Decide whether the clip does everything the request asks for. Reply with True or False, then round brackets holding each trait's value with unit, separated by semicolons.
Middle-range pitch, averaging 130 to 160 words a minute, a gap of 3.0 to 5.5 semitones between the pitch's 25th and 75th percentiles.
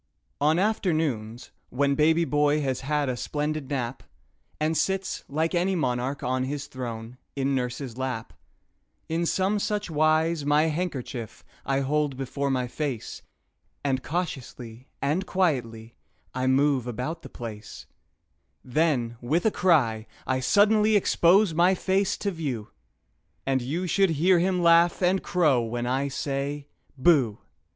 True (145 Hz; 140 wpm; 4.8 semitones)